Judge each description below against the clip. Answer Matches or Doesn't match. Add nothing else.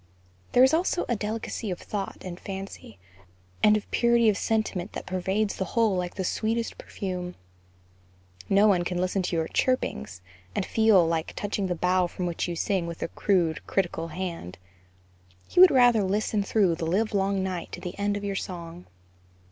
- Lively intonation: Doesn't match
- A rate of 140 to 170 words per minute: Doesn't match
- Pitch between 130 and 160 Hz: Doesn't match